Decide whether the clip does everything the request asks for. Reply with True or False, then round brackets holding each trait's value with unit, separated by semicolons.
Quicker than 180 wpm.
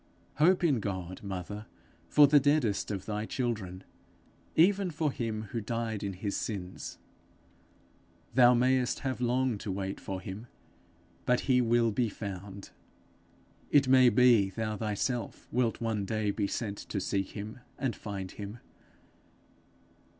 False (140 wpm)